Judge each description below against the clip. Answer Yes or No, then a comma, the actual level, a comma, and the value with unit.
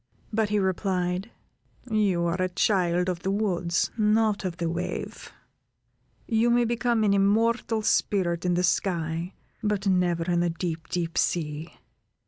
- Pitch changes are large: No, average, 3.4 semitones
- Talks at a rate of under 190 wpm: Yes, average, 145 wpm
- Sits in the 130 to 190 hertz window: Yes, medium, 185 Hz